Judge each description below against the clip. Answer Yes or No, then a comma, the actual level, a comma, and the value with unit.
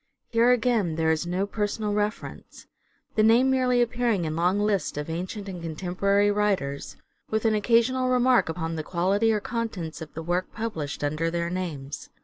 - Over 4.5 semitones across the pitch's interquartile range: Yes, wide, 5.4 semitones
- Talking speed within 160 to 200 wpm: Yes, average, 170 wpm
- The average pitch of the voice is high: Yes, high, 200 Hz